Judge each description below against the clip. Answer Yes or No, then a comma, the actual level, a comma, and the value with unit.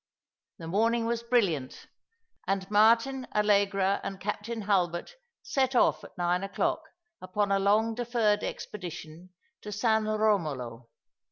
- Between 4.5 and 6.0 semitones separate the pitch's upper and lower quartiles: No, average, 3.6 semitones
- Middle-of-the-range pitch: No, high, 205 Hz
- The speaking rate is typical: No, slow, 120 wpm